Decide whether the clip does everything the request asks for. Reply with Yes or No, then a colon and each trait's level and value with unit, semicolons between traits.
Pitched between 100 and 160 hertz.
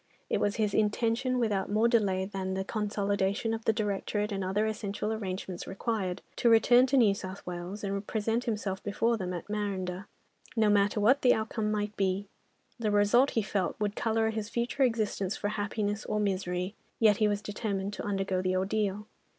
No: high, 205 Hz